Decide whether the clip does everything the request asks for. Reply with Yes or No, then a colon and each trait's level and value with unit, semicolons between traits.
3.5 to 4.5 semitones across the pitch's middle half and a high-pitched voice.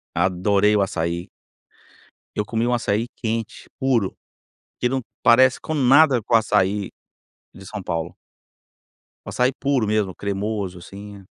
No: average, 3.9 semitones; low, 105 Hz